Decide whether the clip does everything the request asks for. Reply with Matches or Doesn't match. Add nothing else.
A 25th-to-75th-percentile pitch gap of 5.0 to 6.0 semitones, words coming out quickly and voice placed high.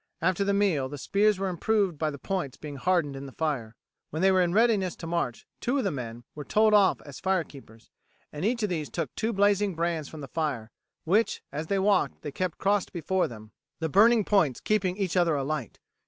Doesn't match